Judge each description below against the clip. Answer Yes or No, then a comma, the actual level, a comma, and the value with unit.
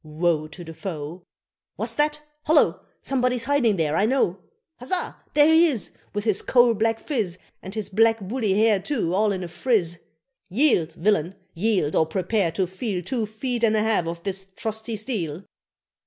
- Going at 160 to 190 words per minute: Yes, average, 175 wpm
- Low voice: No, high, 210 Hz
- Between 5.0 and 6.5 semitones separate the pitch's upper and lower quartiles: Yes, average, 5.3 semitones